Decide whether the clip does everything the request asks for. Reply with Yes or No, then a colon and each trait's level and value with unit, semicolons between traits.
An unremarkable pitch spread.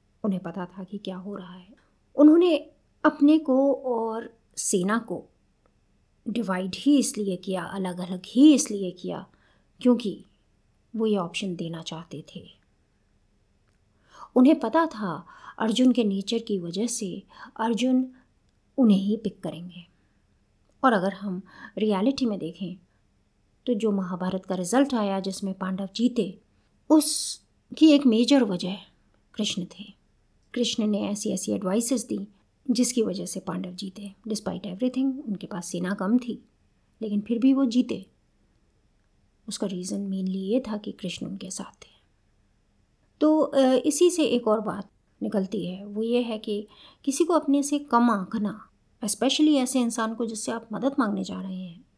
Yes: average, 4.8 semitones